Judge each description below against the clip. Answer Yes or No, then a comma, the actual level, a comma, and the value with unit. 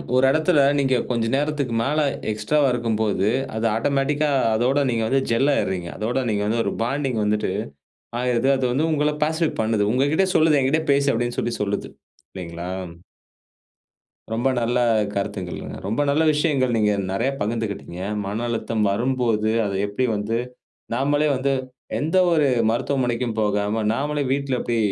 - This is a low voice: Yes, low, 120 Hz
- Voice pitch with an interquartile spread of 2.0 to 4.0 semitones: No, average, 4.6 semitones